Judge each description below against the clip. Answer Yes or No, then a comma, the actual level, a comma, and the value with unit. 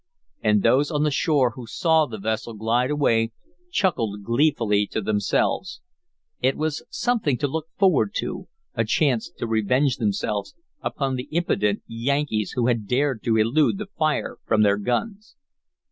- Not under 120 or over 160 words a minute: Yes, average, 155 wpm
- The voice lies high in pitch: No, low, 125 Hz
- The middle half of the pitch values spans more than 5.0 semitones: Yes, wide, 5.5 semitones